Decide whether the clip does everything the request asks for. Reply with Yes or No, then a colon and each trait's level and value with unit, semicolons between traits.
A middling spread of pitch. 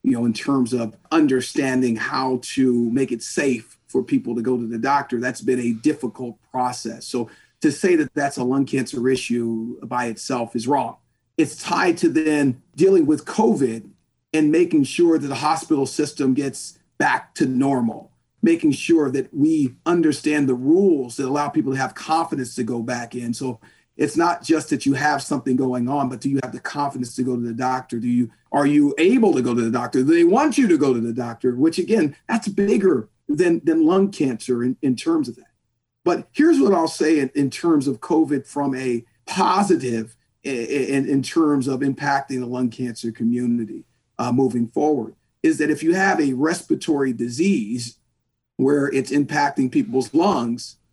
Yes: average, 4.4 semitones